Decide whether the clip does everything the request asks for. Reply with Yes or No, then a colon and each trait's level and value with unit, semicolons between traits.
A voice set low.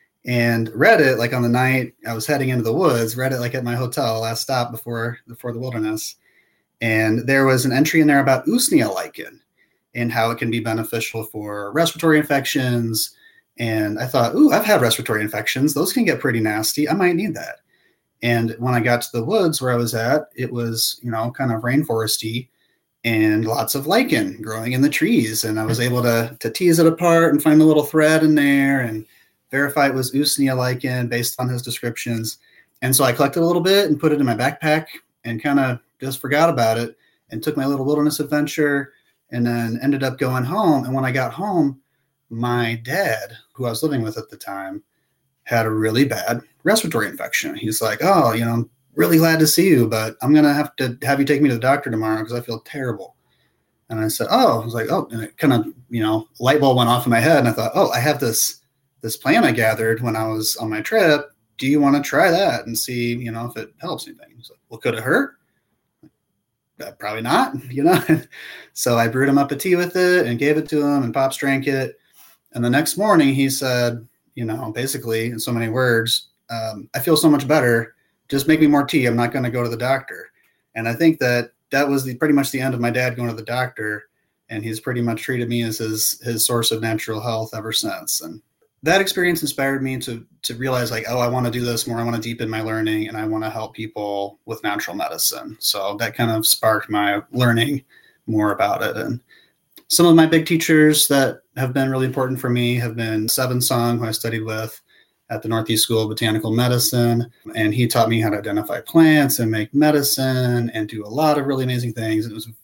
Yes: low, 120 Hz